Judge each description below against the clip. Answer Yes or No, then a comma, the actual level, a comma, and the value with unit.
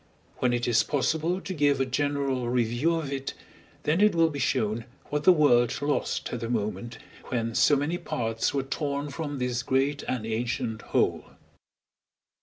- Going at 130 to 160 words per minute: No, average, 170 wpm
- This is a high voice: No, low, 135 Hz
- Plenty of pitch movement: No, average, 3.6 semitones